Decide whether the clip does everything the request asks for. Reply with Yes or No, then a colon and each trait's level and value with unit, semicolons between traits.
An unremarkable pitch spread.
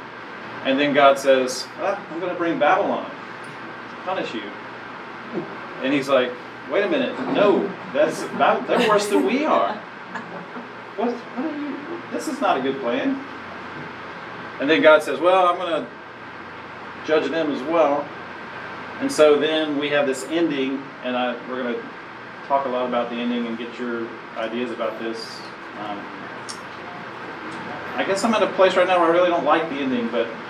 No: wide, 6.9 semitones